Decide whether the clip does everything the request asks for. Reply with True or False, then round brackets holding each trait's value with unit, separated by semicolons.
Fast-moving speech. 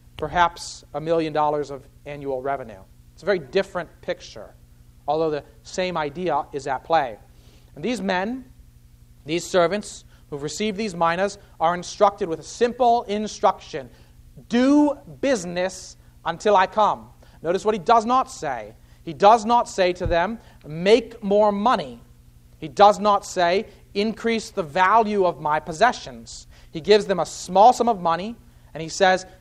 False (155 wpm)